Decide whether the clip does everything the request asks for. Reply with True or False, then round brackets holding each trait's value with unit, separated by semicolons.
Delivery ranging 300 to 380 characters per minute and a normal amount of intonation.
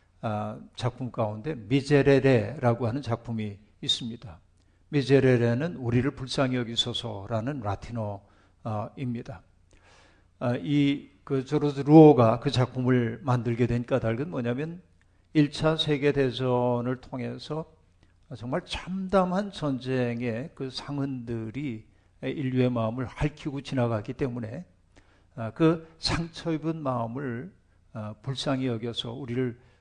False (250 characters per minute; 4.0 semitones)